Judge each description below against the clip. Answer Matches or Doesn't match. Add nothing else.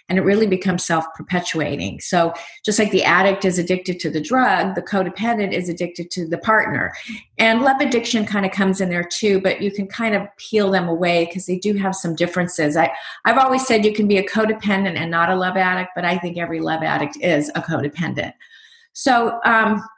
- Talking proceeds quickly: Matches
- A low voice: Doesn't match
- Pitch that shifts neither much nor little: Matches